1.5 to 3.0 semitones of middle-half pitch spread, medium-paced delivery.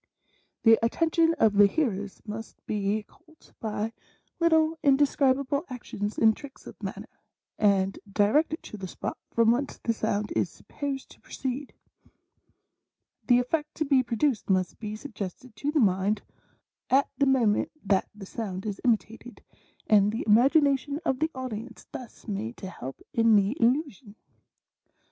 No: average, 5.0 semitones; average, 150 wpm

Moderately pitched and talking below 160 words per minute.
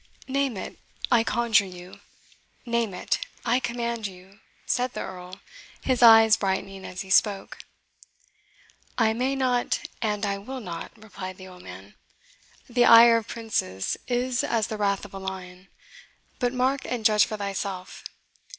No: high, 215 Hz; average, 150 wpm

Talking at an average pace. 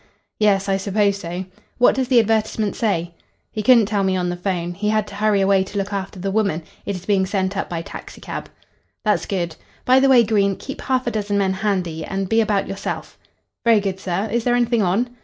No: fast, 220 wpm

